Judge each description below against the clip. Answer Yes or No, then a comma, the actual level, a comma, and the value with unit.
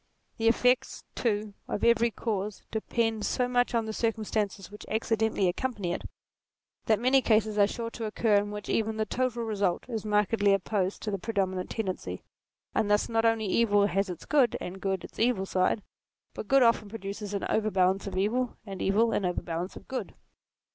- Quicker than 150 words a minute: Yes, average, 185 wpm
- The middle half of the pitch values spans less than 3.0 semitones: Yes, narrow, 2.5 semitones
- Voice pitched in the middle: No, high, 215 Hz